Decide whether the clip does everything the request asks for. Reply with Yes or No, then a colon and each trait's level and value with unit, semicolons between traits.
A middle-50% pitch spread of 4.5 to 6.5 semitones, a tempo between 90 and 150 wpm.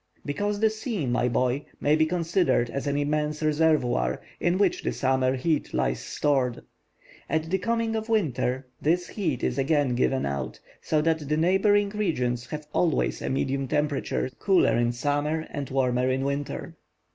No: average, 4.8 semitones; average, 165 wpm